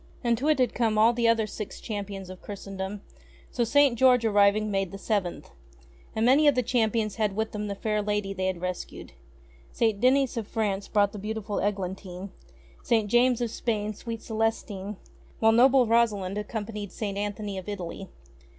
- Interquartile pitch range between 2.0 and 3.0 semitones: Yes, narrow, 2.5 semitones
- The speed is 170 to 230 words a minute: Yes, average, 175 wpm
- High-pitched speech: Yes, high, 210 Hz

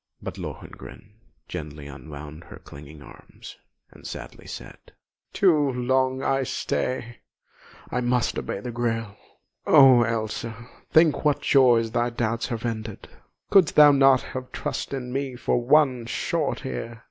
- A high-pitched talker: No, low, 120 Hz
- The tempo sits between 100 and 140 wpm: Yes, slow, 135 wpm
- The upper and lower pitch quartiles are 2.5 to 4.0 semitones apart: Yes, average, 3.1 semitones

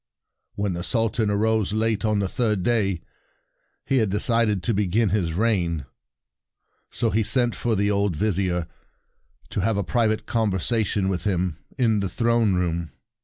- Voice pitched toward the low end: Yes, low, 105 Hz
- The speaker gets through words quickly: No, average, 160 wpm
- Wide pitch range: No, average, 3.2 semitones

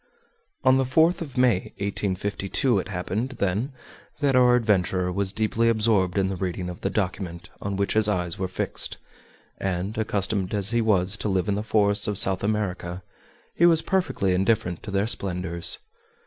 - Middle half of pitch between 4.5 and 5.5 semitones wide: No, average, 3.2 semitones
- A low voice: Yes, low, 100 Hz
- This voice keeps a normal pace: Yes, average, 175 wpm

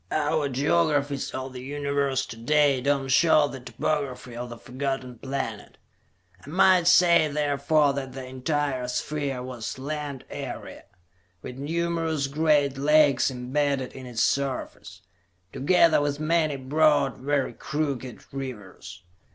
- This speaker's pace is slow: Yes, slow, 130 wpm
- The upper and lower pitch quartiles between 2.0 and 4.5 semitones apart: Yes, narrow, 2.5 semitones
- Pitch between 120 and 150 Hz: Yes, medium, 140 Hz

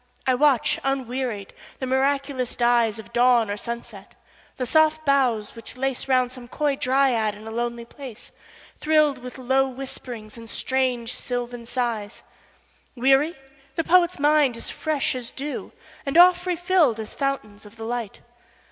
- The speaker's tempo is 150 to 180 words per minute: No, slow, 135 wpm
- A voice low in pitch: No, very high, 255 Hz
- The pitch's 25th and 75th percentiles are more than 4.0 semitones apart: No, average, 2.9 semitones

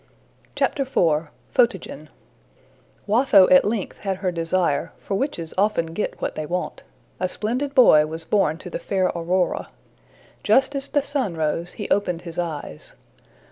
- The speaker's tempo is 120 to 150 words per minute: Yes, average, 145 wpm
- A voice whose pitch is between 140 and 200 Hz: Yes, medium, 185 Hz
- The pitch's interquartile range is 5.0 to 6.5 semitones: Yes, wide, 5.5 semitones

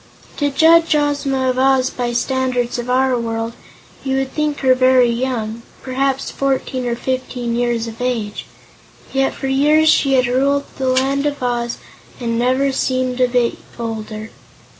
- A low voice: No, very high, 255 Hz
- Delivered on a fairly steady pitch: Yes, narrow, 2.0 semitones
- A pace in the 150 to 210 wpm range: Yes, average, 165 wpm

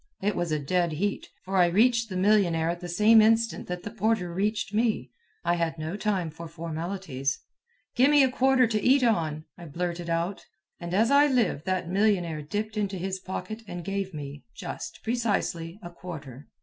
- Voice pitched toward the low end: No, medium, 185 Hz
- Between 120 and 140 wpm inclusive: No, average, 185 wpm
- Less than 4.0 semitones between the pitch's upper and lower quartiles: No, average, 4.3 semitones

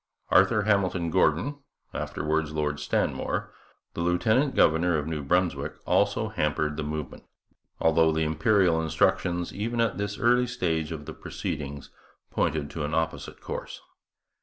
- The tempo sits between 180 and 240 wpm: No, slow, 135 wpm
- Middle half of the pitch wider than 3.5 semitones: Yes, average, 4.4 semitones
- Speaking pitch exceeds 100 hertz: No, very low, 80 Hz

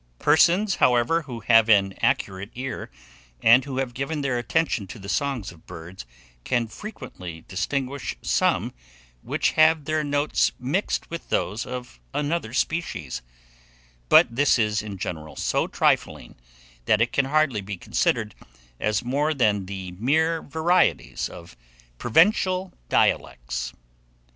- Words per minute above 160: No, slow, 135 wpm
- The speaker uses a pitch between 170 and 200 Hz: No, low, 125 Hz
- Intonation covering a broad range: Yes, wide, 7.3 semitones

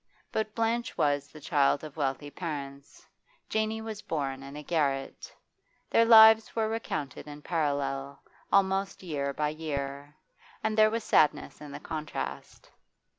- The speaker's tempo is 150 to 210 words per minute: No, average, 140 wpm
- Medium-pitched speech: Yes, medium, 150 Hz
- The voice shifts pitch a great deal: Yes, wide, 7.4 semitones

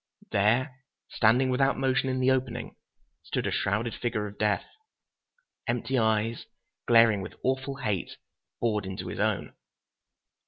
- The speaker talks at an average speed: No, slow, 130 wpm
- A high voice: No, low, 115 Hz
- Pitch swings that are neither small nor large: Yes, average, 3.6 semitones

